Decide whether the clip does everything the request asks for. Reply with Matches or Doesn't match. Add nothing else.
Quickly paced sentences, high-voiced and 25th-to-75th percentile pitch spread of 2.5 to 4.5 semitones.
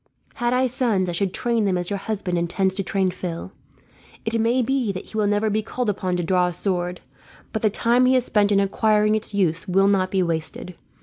Matches